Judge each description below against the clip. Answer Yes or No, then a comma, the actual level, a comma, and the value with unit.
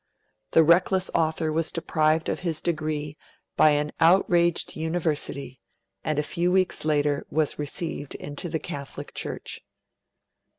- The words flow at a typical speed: No, slow, 130 wpm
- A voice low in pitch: No, medium, 155 Hz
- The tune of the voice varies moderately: No, narrow, 2.3 semitones